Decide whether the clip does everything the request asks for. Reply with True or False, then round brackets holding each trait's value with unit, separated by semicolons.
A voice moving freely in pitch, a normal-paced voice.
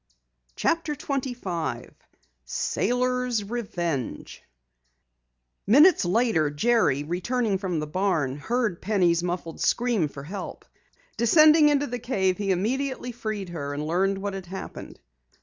False (6.1 semitones; 115 wpm)